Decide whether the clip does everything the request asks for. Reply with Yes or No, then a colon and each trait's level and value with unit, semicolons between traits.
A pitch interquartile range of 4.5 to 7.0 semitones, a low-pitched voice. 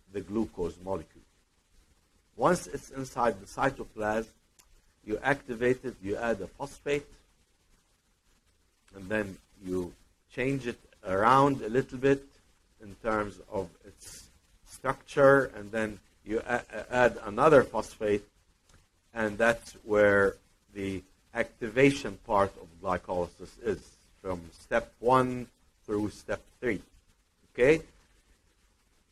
Yes: average, 5.3 semitones; low, 100 Hz